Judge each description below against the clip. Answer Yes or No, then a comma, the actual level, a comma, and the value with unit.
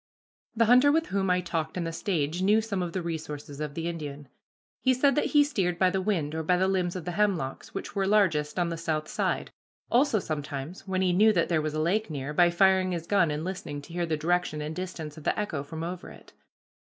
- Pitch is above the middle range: No, medium, 175 Hz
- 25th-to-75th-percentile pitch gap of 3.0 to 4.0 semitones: Yes, average, 3.7 semitones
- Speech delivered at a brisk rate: Yes, fast, 240 wpm